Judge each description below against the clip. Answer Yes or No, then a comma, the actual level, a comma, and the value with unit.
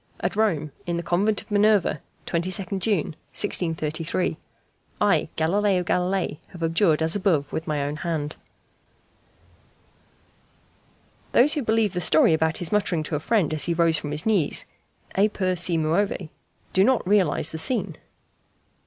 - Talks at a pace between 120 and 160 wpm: Yes, average, 150 wpm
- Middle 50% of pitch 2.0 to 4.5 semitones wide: Yes, average, 4.2 semitones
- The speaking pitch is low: No, medium, 175 Hz